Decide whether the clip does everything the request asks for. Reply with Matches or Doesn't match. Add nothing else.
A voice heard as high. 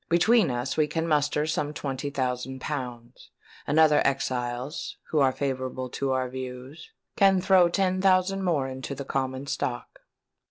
Doesn't match